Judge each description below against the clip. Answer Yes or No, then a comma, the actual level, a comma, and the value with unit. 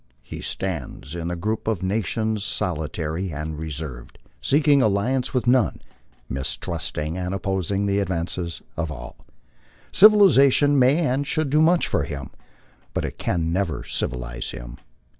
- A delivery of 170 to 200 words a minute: No, average, 140 wpm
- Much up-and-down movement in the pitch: Yes, wide, 7.9 semitones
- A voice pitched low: Yes, very low, 95 Hz